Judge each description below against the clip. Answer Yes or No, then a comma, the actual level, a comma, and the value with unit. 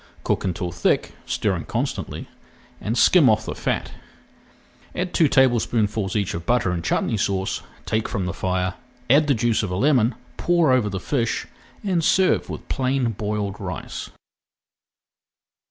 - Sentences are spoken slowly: No, average, 150 wpm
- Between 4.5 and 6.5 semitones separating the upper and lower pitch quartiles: Yes, wide, 5.5 semitones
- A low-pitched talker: Yes, low, 110 Hz